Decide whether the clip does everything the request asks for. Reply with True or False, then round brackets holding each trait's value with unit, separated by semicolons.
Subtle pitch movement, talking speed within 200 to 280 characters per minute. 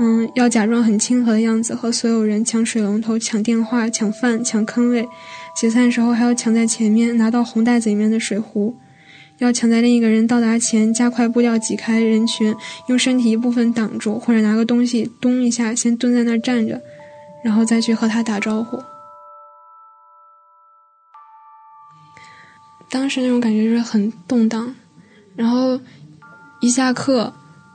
True (1.9 semitones; 245 characters per minute)